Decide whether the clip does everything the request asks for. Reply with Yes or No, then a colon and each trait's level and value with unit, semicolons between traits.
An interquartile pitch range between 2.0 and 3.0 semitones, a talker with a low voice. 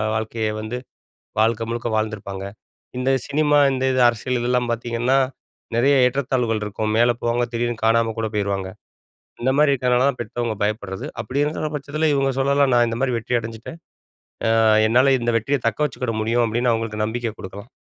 Yes: narrow, 2.6 semitones; low, 120 Hz